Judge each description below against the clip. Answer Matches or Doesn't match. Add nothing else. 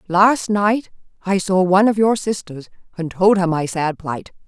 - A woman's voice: Matches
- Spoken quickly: Doesn't match